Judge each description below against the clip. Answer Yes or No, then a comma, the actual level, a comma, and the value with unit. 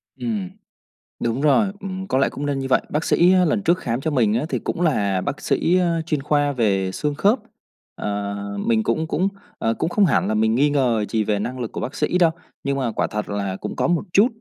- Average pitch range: No, wide, 7.3 semitones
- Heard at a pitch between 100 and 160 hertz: Yes, medium, 140 Hz